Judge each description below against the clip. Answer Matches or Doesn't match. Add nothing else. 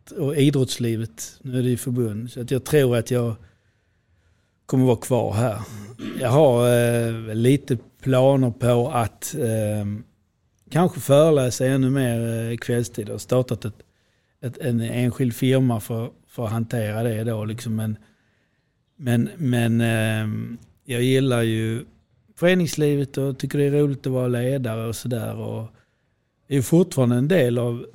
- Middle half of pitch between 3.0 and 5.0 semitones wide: Doesn't match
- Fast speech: Doesn't match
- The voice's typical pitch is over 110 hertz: Matches